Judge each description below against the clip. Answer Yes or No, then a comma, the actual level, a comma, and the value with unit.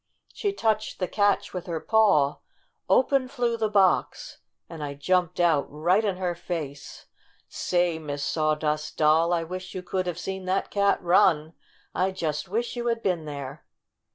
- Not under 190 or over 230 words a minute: No, average, 165 wpm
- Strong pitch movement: No, average, 4.4 semitones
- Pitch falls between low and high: Yes, medium, 180 Hz